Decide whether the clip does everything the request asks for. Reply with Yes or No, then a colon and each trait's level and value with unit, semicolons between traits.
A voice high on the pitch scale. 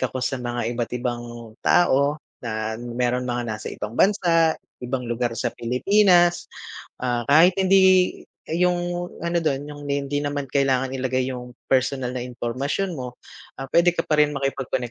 No: low, 135 Hz